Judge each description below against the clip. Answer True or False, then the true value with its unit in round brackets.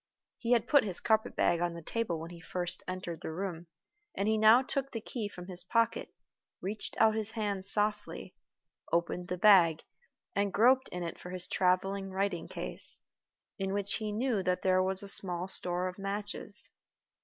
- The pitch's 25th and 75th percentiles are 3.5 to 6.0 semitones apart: False (3.1 semitones)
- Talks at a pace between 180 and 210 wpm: True (185 wpm)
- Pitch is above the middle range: True (195 Hz)